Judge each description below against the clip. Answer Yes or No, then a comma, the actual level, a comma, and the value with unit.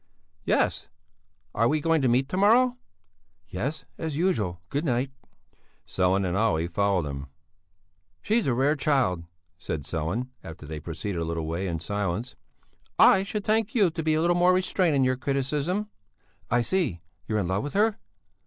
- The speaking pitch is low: Yes, low, 130 Hz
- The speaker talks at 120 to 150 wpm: No, average, 170 wpm